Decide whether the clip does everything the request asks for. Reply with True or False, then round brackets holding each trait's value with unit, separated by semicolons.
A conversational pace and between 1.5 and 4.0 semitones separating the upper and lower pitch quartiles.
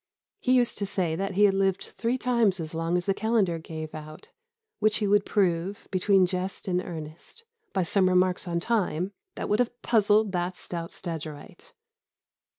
True (175 wpm; 3.4 semitones)